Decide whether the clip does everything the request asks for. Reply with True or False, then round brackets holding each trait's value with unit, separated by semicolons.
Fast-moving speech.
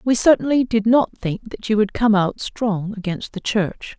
True (210 wpm)